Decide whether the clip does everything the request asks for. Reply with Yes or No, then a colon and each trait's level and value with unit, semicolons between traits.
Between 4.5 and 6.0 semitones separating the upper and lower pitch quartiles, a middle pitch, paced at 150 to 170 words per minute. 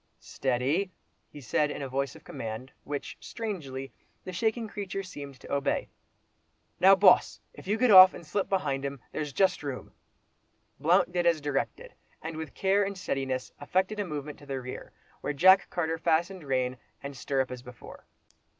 Yes: wide, 5.6 semitones; medium, 150 Hz; average, 165 wpm